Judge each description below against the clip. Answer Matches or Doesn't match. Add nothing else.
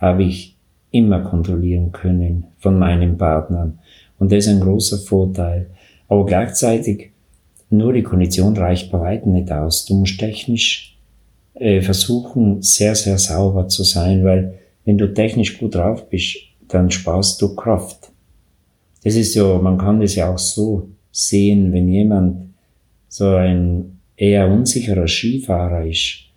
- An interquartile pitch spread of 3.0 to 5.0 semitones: Doesn't match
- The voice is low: Matches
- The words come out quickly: Doesn't match